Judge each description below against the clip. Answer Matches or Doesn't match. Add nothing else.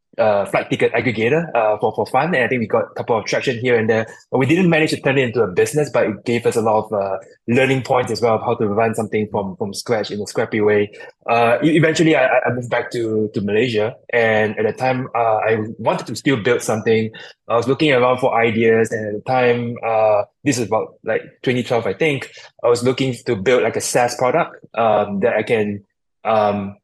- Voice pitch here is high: Doesn't match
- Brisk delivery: Matches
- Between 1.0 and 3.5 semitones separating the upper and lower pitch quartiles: Matches